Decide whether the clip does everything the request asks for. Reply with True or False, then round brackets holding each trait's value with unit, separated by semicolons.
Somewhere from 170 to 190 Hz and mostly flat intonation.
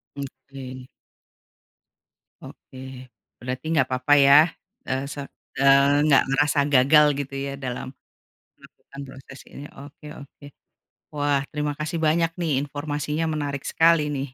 False (140 Hz; 1.6 semitones)